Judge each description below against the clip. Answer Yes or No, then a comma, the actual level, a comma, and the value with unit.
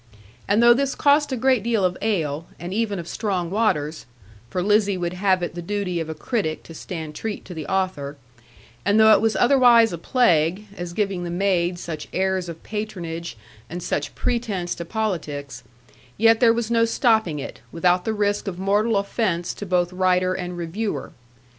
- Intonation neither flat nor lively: Yes, average, 4.2 semitones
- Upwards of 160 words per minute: Yes, average, 185 wpm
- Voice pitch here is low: No, high, 190 Hz